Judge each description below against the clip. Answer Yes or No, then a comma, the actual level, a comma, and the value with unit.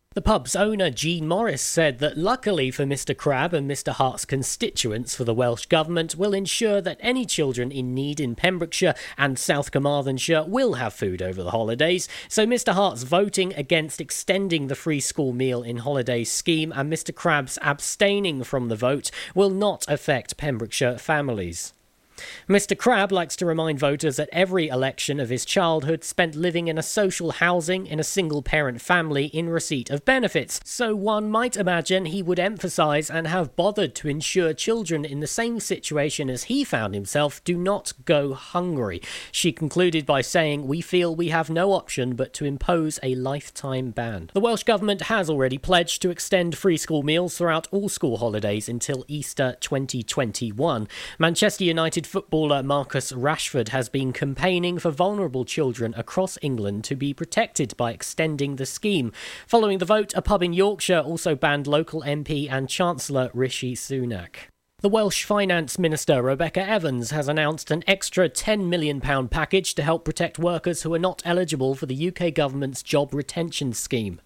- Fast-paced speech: No, average, 170 wpm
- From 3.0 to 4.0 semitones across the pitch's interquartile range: No, average, 5.2 semitones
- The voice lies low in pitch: No, medium, 155 Hz